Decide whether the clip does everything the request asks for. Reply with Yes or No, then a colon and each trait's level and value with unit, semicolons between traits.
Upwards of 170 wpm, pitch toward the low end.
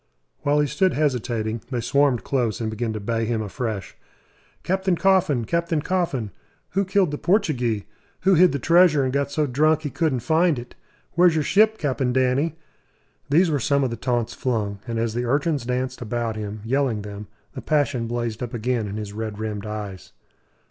Yes: average, 185 wpm; low, 130 Hz